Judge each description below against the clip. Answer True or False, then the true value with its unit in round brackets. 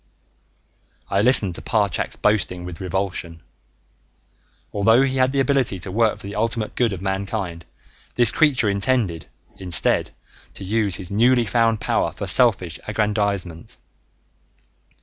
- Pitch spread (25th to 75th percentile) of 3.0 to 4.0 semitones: True (3.5 semitones)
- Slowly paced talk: True (130 wpm)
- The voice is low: True (105 Hz)